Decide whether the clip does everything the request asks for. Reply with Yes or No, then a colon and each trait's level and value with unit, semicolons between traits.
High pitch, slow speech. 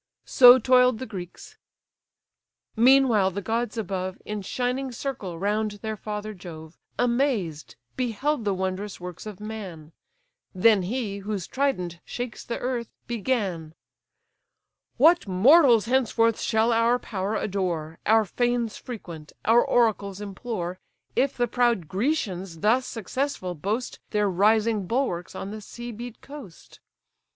Yes: high, 215 Hz; slow, 125 wpm